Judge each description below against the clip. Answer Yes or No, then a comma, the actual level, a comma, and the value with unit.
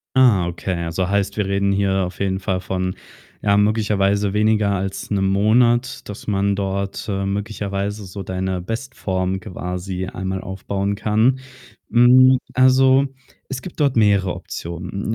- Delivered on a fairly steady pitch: Yes, narrow, 2.2 semitones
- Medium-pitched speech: No, low, 100 Hz